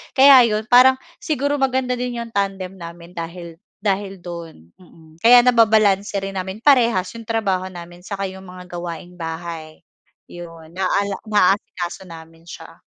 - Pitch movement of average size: Yes, average, 4.7 semitones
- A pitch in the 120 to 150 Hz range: No, high, 190 Hz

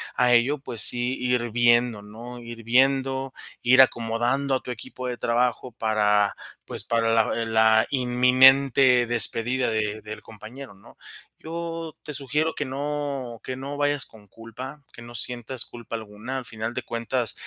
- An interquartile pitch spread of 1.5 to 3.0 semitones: Yes, average, 2.7 semitones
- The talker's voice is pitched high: No, low, 125 Hz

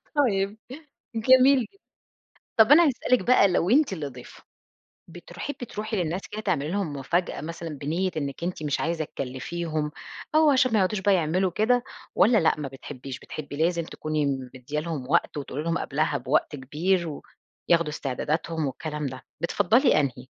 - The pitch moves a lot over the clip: Yes, wide, 5.7 semitones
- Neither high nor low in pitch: Yes, medium, 170 Hz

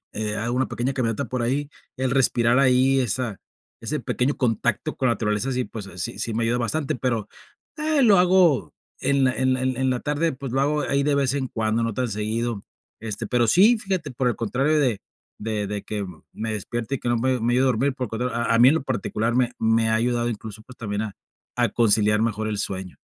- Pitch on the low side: Yes, low, 120 Hz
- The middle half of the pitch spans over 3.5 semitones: No, average, 3.2 semitones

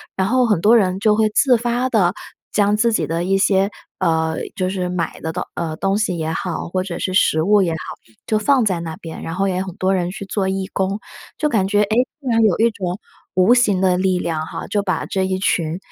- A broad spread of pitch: No, average, 2.9 semitones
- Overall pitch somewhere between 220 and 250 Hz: No, high, 190 Hz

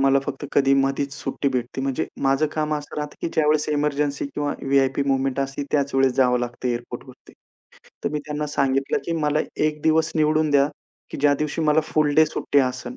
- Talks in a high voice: No, medium, 140 Hz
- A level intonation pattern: Yes, narrow, 1.8 semitones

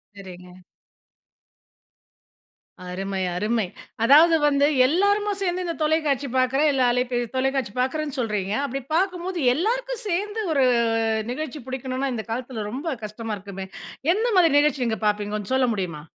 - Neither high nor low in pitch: No, very high, 260 Hz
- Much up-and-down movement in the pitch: Yes, wide, 7.3 semitones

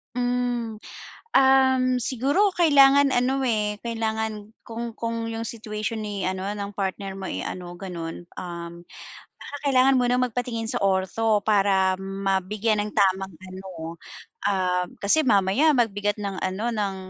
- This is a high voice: Yes, high, 215 Hz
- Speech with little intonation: No, average, 4.2 semitones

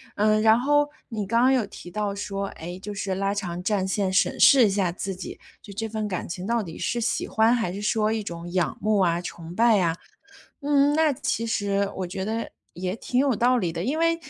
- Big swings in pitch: No, average, 3.8 semitones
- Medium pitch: No, high, 210 Hz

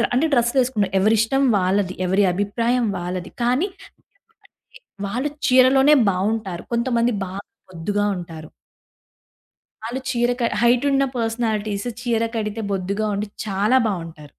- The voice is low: No, high, 225 Hz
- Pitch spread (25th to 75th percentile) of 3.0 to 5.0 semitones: Yes, average, 4.2 semitones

